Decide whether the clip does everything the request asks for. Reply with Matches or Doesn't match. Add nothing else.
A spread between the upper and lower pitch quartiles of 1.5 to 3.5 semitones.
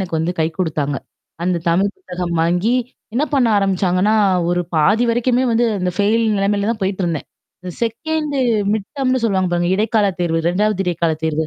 Doesn't match